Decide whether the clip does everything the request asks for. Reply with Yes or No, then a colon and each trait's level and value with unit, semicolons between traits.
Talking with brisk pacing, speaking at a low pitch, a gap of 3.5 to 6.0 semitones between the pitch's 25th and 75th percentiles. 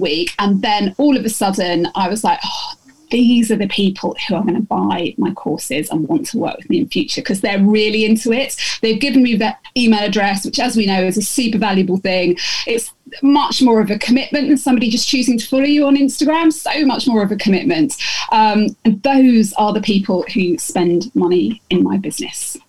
No: fast, 220 wpm; high, 230 Hz; average, 5.2 semitones